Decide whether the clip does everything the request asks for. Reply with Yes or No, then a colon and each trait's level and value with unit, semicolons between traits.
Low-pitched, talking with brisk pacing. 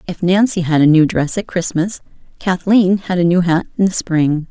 No: medium, 175 Hz; fast, 215 wpm